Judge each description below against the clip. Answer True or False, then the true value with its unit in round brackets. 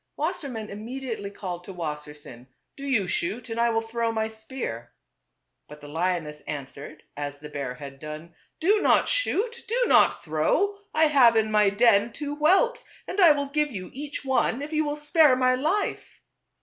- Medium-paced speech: True (185 wpm)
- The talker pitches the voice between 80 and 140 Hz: False (225 Hz)